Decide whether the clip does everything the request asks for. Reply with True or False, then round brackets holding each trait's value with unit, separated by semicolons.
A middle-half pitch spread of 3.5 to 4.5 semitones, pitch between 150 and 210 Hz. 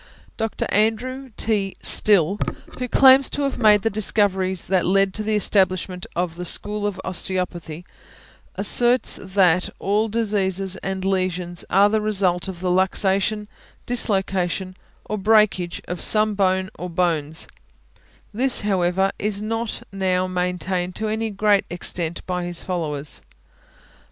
False (2.8 semitones; 190 Hz)